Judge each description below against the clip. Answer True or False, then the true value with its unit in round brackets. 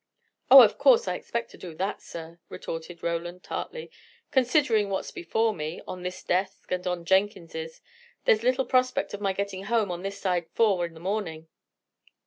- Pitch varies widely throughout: False (4.1 semitones)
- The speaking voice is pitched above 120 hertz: True (190 Hz)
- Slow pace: False (175 wpm)